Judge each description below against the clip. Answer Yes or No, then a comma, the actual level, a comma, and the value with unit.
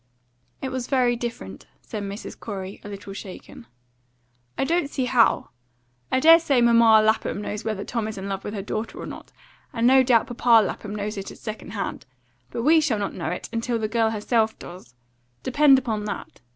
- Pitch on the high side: Yes, high, 225 Hz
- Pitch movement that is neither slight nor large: Yes, average, 3.3 semitones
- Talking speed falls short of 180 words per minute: No, average, 195 wpm